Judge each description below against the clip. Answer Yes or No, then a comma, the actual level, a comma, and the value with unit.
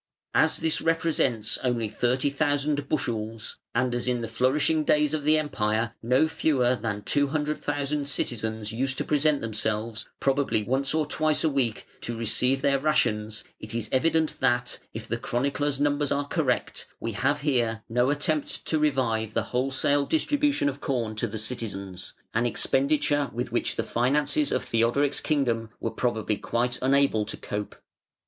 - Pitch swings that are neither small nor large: Yes, average, 4.2 semitones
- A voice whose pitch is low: Yes, low, 130 Hz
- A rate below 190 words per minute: Yes, average, 155 wpm